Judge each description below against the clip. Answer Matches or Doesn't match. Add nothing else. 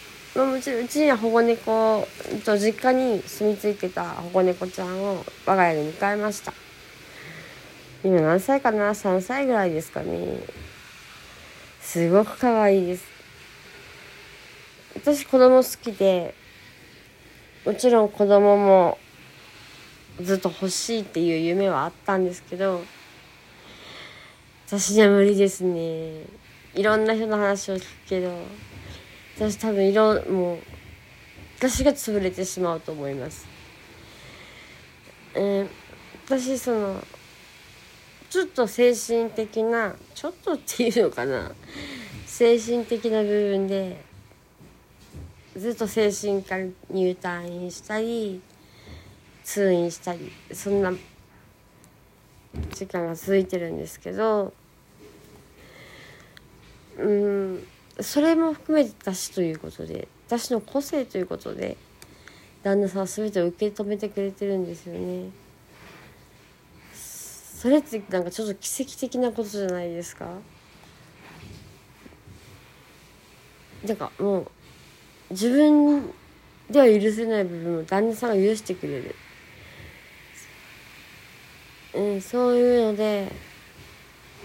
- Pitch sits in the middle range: Doesn't match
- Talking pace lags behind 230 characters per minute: Matches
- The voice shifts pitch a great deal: Doesn't match